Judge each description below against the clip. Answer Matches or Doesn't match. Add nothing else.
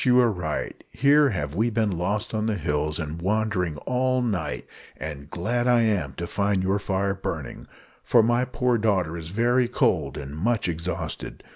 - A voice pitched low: Matches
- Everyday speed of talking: Matches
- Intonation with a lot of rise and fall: Matches